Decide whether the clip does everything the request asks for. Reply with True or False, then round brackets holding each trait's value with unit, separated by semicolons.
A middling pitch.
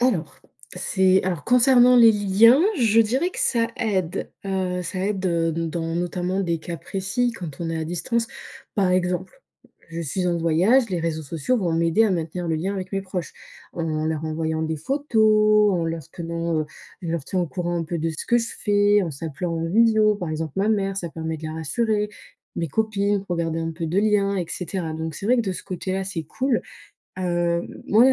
True (180 Hz)